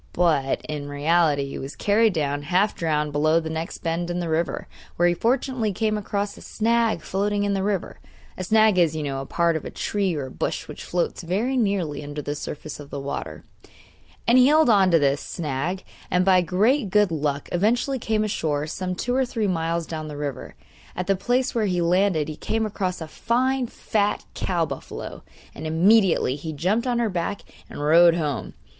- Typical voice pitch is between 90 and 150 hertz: No, medium, 180 Hz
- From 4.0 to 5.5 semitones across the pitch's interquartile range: Yes, average, 5.2 semitones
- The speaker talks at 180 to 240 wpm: Yes, average, 200 wpm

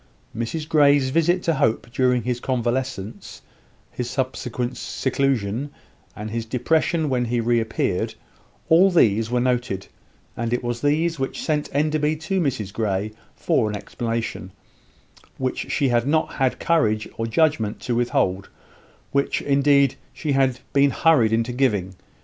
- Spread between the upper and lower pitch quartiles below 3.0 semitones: No, average, 4.0 semitones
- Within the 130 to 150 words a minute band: Yes, average, 140 wpm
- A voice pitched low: Yes, low, 125 Hz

